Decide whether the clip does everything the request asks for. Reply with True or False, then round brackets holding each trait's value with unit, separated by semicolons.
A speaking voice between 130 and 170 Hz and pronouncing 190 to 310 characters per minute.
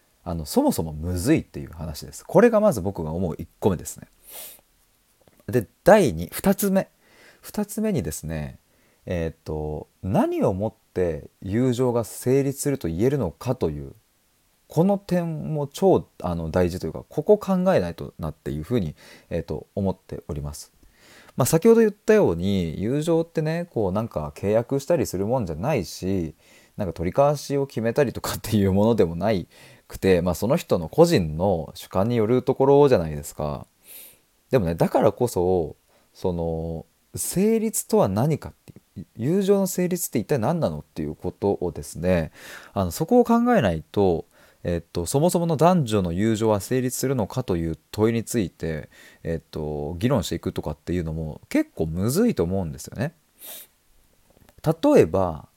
False (110 Hz; 300 characters per minute)